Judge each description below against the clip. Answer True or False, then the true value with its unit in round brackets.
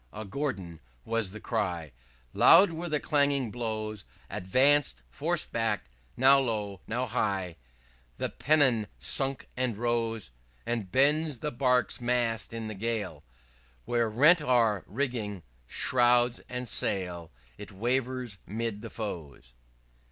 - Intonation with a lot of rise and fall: False (4.0 semitones)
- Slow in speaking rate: True (125 wpm)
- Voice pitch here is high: False (115 Hz)